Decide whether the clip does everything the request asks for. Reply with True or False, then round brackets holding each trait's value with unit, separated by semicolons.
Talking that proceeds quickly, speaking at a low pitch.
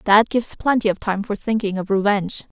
False (210 wpm; 205 Hz)